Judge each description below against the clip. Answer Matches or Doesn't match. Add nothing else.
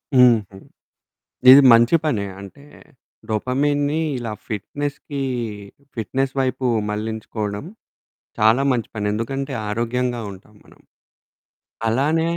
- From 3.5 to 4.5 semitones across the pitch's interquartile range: Matches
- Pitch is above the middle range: Doesn't match